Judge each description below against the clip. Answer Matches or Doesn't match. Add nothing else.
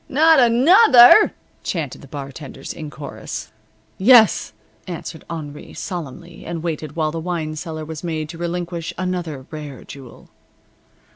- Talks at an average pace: Doesn't match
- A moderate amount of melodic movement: Matches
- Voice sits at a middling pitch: Matches